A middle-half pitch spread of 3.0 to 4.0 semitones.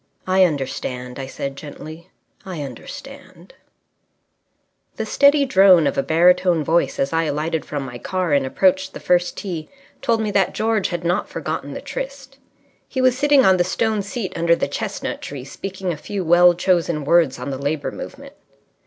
No: average, 4.6 semitones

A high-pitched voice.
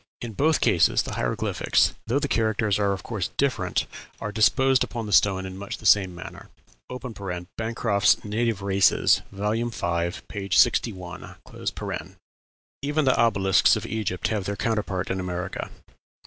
No: low, 105 Hz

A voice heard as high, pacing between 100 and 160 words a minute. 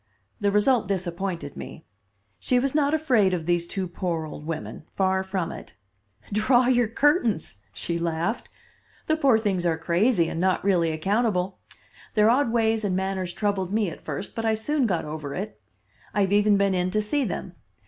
No: high, 195 Hz; average, 180 wpm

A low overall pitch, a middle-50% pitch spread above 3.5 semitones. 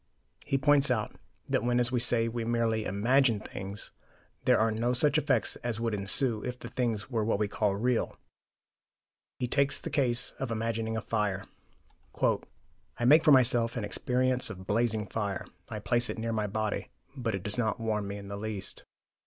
No: low, 115 Hz; average, 2.7 semitones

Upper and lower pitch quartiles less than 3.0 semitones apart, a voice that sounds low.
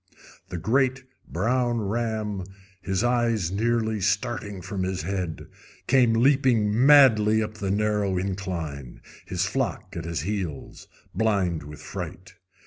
No: average, 4.1 semitones; low, 105 Hz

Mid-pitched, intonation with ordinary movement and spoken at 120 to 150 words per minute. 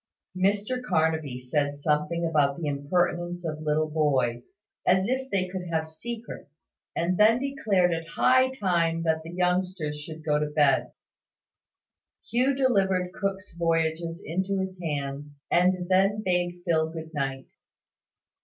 Yes: medium, 170 Hz; average, 3.6 semitones; slow, 135 wpm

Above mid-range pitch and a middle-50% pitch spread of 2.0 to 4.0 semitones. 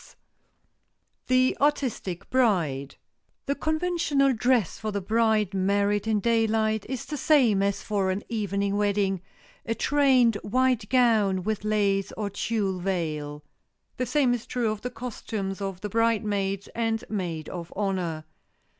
Yes: high, 210 Hz; average, 3.7 semitones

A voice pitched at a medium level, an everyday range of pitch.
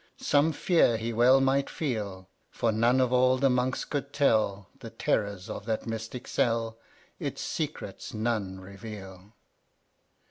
No: low, 115 Hz; average, 3.7 semitones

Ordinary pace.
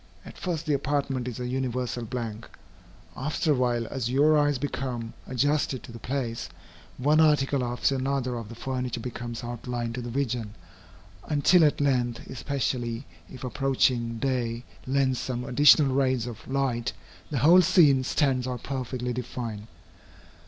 Yes: average, 150 wpm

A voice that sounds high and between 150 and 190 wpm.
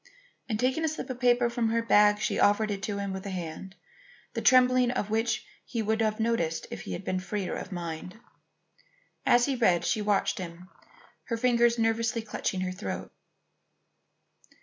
Yes: high, 220 Hz; average, 175 wpm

